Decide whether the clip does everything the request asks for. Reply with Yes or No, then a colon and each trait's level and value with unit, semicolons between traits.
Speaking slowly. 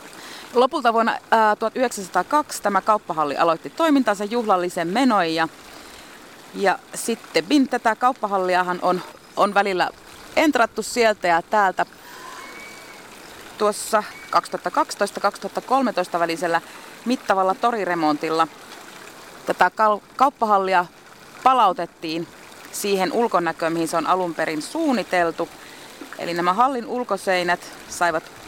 Yes: slow, 90 wpm